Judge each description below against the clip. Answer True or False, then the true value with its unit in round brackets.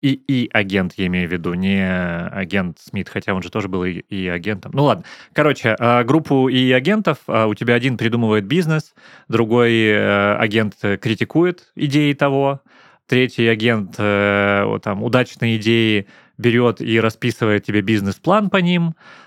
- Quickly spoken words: False (145 wpm)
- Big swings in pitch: False (4.8 semitones)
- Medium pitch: False (115 Hz)